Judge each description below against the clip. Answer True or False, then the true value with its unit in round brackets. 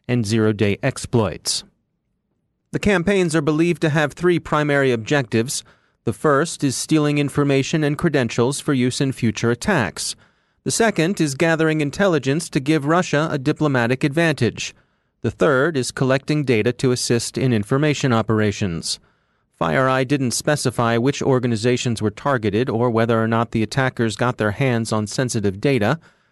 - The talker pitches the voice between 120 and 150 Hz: True (135 Hz)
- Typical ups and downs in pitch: True (4.4 semitones)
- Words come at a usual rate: True (150 wpm)